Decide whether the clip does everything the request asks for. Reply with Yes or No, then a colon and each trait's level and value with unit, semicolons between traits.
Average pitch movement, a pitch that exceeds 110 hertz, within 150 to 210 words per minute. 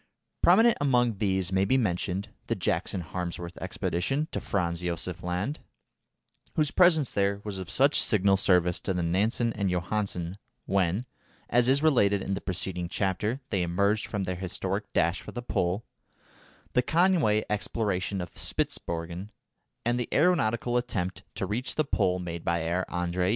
No: average, 4.8 semitones; very low, 95 Hz; average, 155 wpm